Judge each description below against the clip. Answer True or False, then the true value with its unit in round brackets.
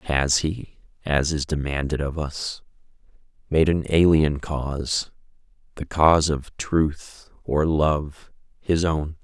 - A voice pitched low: True (75 Hz)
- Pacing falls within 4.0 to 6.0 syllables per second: False (3.6 syllables/s)